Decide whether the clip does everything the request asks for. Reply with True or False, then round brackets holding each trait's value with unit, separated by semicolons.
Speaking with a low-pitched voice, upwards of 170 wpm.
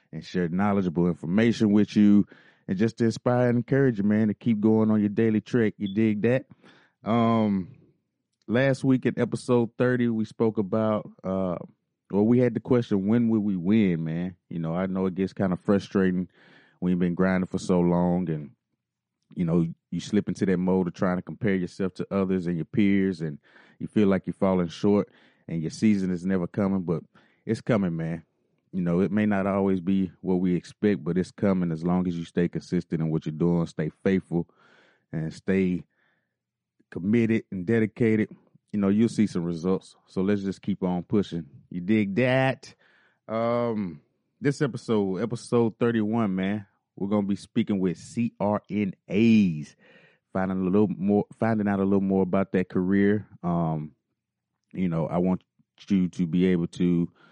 True (95 Hz; 180 wpm)